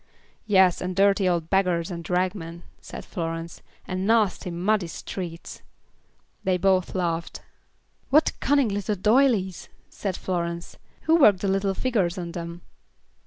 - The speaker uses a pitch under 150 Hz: No, medium, 185 Hz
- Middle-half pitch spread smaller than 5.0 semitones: Yes, average, 2.9 semitones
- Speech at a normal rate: No, slow, 130 wpm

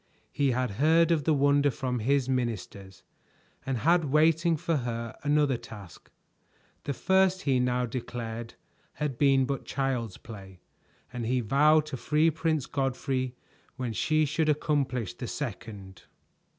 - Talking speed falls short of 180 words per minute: Yes, average, 140 wpm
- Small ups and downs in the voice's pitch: No, average, 4.2 semitones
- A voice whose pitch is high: No, low, 135 Hz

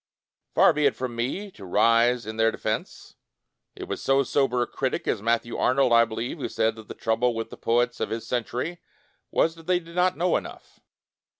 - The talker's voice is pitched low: Yes, low, 120 Hz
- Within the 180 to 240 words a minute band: Yes, fast, 205 wpm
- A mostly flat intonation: No, average, 3.8 semitones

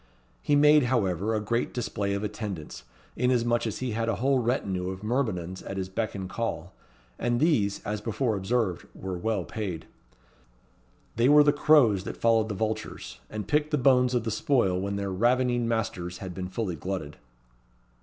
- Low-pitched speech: Yes, low, 110 Hz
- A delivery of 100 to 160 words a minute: No, average, 175 wpm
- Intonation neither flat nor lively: Yes, average, 4.4 semitones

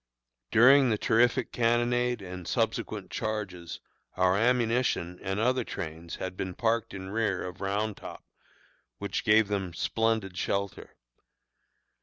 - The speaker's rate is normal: No, slow, 125 wpm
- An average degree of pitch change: Yes, average, 4.0 semitones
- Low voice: Yes, low, 105 Hz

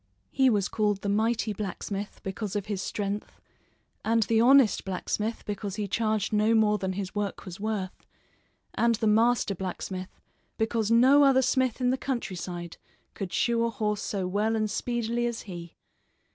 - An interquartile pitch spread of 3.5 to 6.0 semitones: No, average, 2.8 semitones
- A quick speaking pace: No, average, 165 wpm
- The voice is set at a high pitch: Yes, high, 215 Hz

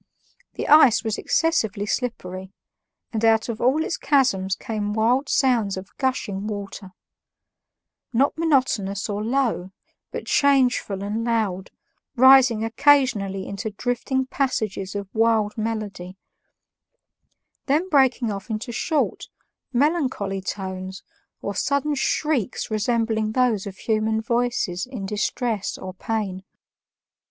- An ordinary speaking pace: No, slow, 115 wpm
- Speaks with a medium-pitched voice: No, high, 220 Hz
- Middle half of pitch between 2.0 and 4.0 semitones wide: No, average, 4.4 semitones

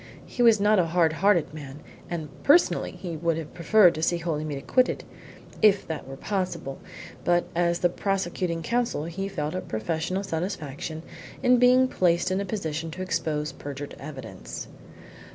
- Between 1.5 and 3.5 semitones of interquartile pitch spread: No, average, 4.0 semitones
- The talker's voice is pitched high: No, medium, 170 Hz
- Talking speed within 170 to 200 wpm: No, average, 160 wpm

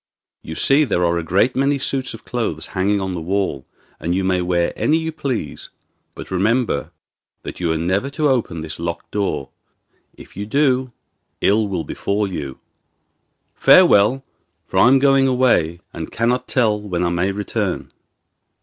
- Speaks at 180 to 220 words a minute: No, average, 170 wpm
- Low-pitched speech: Yes, low, 100 Hz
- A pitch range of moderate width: No, wide, 6.8 semitones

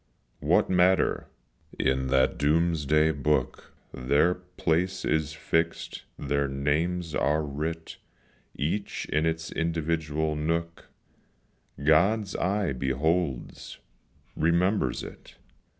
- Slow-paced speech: Yes, slow, 95 wpm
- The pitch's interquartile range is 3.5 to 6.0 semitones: No, average, 2.8 semitones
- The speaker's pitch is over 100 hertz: No, very low, 80 Hz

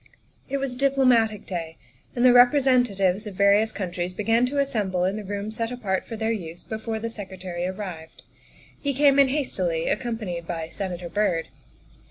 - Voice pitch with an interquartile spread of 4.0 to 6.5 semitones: Yes, average, 5.1 semitones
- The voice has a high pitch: Yes, high, 210 Hz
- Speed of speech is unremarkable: Yes, average, 165 wpm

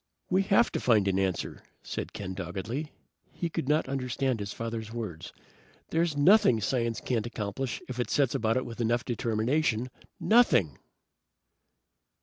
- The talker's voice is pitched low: Yes, low, 120 Hz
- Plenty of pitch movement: No, average, 4.2 semitones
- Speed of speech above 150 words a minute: No, average, 145 wpm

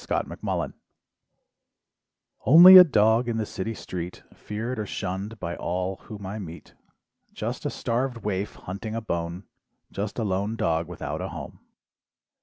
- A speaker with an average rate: Yes, average, 150 wpm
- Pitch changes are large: No, average, 3.5 semitones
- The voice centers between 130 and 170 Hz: No, low, 105 Hz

